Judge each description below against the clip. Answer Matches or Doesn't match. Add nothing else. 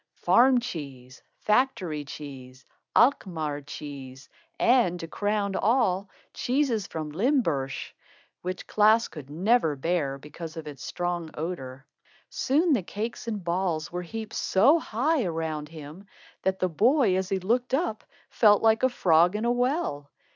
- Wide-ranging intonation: Matches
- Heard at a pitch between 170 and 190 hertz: Matches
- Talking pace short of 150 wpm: Matches